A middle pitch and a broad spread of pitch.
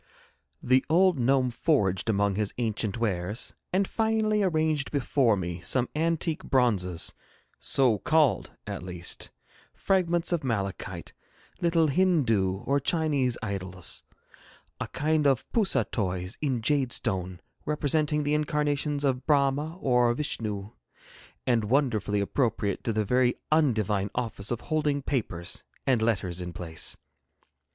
No: low, 125 Hz; wide, 6.7 semitones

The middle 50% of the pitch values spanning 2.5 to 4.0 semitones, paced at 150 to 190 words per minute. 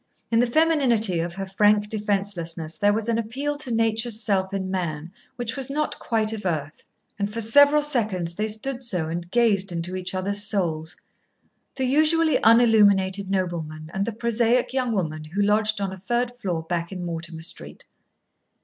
No: average, 4.6 semitones; average, 175 wpm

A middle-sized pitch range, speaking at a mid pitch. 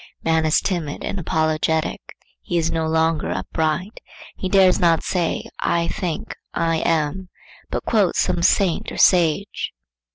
No: narrow, 2.3 semitones; medium, 165 Hz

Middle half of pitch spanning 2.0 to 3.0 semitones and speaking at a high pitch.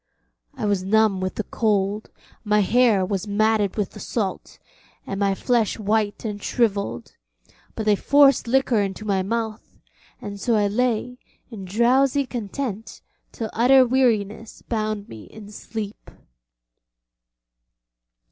Yes: narrow, 2.6 semitones; high, 215 Hz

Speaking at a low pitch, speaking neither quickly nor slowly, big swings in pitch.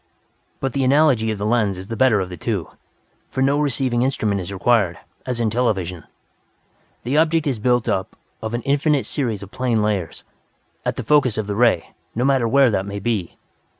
No: low, 115 Hz; average, 195 wpm; average, 4.6 semitones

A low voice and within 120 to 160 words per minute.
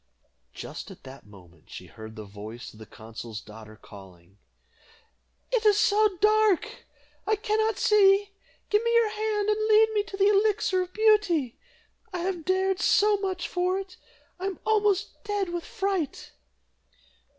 No: very high, 390 Hz; average, 155 wpm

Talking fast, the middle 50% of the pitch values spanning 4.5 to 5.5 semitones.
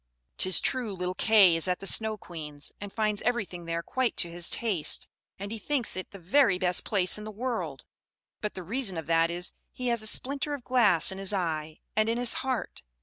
Yes: fast, 215 wpm; average, 4.8 semitones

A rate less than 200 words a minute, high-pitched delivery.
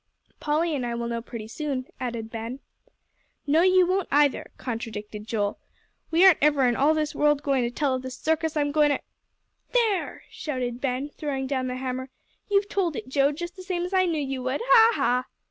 No: fast, 205 wpm; very high, 280 Hz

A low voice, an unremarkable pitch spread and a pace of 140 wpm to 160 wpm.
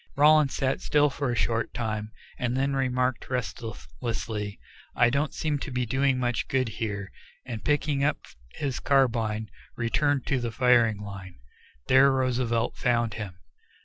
Yes: low, 125 Hz; average, 3.4 semitones; average, 145 wpm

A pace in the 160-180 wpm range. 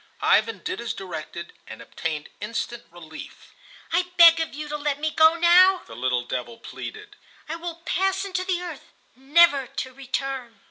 Yes: average, 170 wpm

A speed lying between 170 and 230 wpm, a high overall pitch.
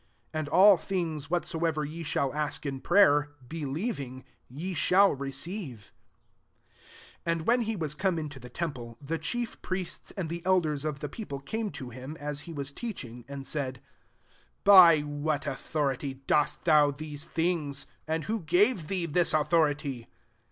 No: average, 175 wpm; medium, 155 Hz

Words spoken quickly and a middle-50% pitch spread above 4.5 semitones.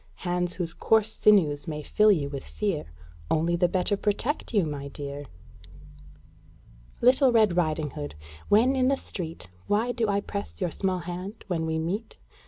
No: average, 165 wpm; average, 4.9 semitones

